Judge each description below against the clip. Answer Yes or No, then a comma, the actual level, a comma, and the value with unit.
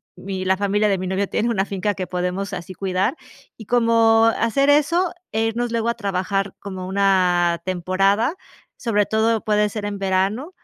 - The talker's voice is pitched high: Yes, high, 200 Hz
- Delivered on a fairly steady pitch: No, average, 3.1 semitones